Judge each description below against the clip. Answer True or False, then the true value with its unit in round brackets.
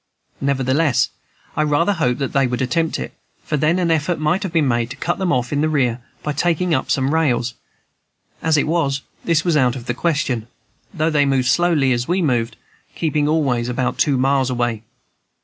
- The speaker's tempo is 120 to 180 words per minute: False (200 wpm)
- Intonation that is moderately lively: True (4.3 semitones)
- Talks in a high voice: False (145 Hz)